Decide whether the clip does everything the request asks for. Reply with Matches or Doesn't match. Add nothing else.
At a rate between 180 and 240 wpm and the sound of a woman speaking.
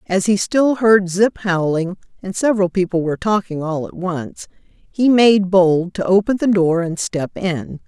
Matches